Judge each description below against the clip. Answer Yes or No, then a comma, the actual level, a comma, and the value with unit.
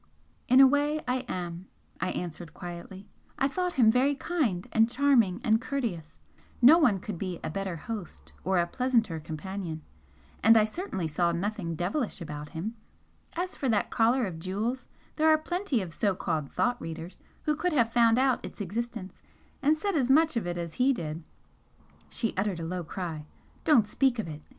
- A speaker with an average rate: Yes, average, 185 wpm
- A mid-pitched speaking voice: No, high, 215 Hz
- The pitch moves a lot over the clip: Yes, wide, 7.1 semitones